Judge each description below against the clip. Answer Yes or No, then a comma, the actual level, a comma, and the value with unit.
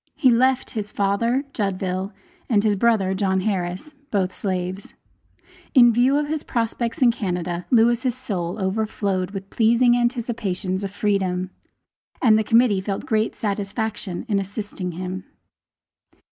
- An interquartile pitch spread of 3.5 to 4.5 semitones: Yes, average, 3.8 semitones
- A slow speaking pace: Yes, slow, 130 wpm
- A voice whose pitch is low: No, high, 205 Hz